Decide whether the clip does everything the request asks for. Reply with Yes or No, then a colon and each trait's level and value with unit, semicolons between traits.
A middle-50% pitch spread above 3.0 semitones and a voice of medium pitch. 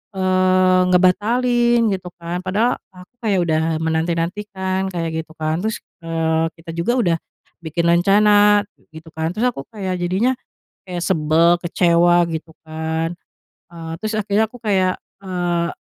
Yes: average, 3.4 semitones; medium, 180 Hz